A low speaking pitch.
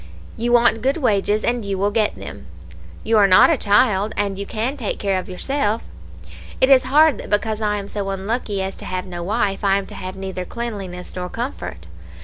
No: high, 205 Hz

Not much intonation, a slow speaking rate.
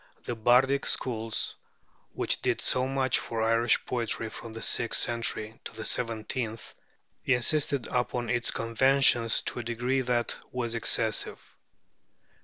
Yes: narrow, 1.9 semitones; slow, 130 wpm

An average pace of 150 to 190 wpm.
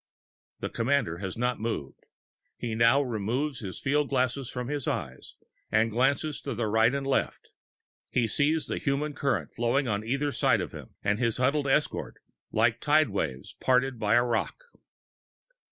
Yes: average, 165 wpm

